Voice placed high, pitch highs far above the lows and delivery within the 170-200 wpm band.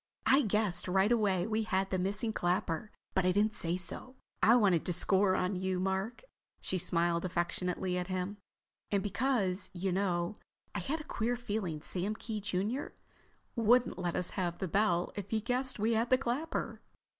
No: high, 195 Hz; average, 3.4 semitones; average, 175 wpm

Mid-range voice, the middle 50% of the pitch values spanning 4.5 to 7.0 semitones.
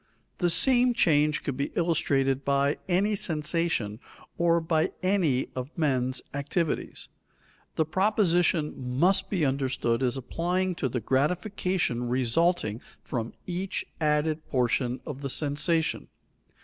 Yes: medium, 150 Hz; average, 4.9 semitones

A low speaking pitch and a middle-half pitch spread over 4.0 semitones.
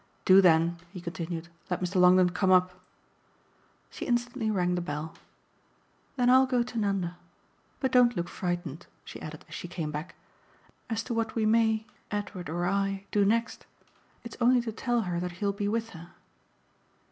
No: high, 195 Hz; average, 4.5 semitones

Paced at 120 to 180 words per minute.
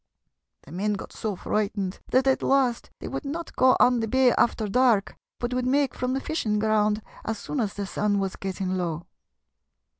No: average, 190 wpm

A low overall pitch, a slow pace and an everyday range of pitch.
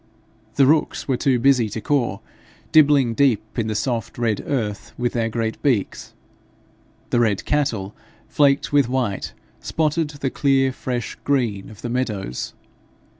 No: low, 125 Hz; average, 145 wpm; average, 4.0 semitones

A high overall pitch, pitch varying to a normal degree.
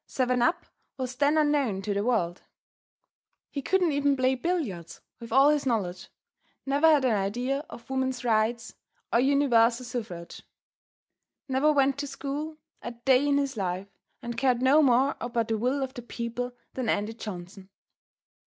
Yes: very high, 250 Hz; average, 3.6 semitones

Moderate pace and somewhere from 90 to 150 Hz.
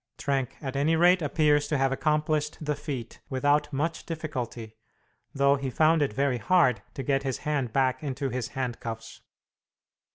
Yes: average, 160 wpm; medium, 140 Hz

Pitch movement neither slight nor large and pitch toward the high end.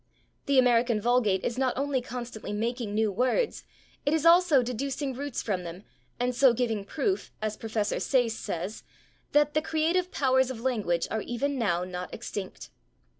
Yes: average, 4.4 semitones; high, 245 Hz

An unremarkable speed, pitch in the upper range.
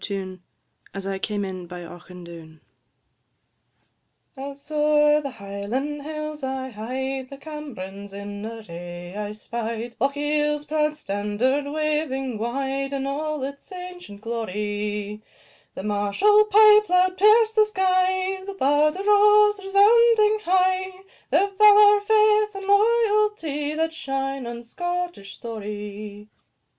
No: slow, 120 wpm; very high, 280 Hz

